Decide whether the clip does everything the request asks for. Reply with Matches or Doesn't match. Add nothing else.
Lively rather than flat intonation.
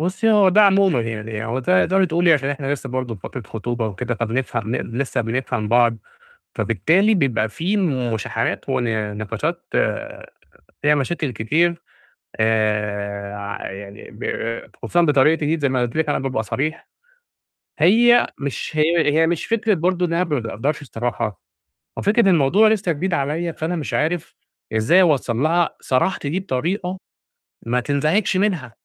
Matches